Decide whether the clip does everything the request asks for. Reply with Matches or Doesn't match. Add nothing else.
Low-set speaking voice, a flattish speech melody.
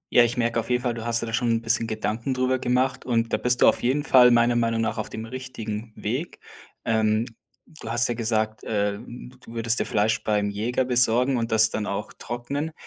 Matches